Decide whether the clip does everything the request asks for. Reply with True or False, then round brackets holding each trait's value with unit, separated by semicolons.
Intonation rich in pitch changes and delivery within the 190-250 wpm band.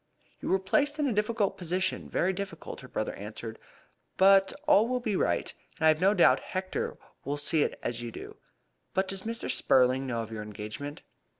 True (7.5 semitones; 195 wpm)